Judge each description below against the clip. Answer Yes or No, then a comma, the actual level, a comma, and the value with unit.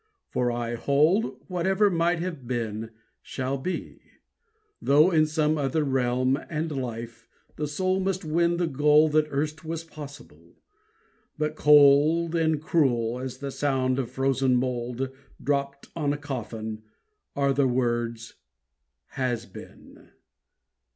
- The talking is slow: Yes, slow, 130 wpm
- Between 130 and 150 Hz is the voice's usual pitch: Yes, medium, 140 Hz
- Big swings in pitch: No, average, 3.7 semitones